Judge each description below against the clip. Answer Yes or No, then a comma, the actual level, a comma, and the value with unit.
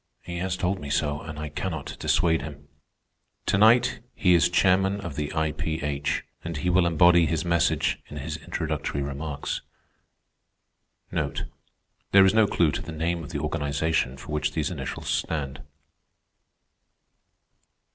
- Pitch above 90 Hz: No, very low, 80 Hz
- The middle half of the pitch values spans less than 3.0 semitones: No, average, 3.3 semitones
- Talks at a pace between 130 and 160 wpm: Yes, average, 145 wpm